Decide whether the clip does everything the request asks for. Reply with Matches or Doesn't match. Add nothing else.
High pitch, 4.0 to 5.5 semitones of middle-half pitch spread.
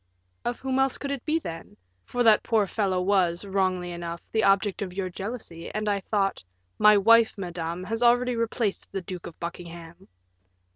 Matches